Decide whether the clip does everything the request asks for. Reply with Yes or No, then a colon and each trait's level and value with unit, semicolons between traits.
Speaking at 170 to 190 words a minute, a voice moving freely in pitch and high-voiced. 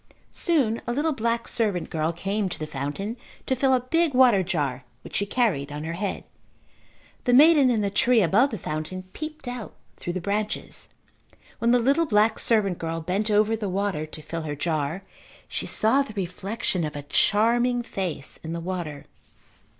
Yes: average, 180 wpm; wide, 6.3 semitones; high, 205 Hz